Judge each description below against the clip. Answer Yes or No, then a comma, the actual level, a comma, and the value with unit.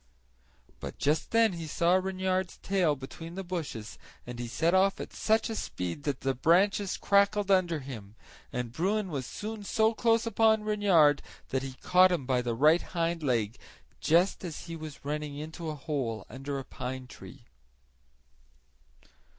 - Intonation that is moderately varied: No, wide, 6.1 semitones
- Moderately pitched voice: Yes, medium, 165 Hz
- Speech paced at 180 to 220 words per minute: No, average, 165 wpm